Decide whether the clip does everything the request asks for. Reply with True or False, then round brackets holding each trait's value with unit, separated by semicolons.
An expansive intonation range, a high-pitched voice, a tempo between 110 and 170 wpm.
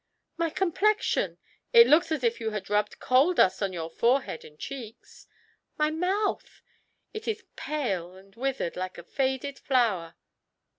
True (8.5 semitones; 255 Hz; 160 wpm)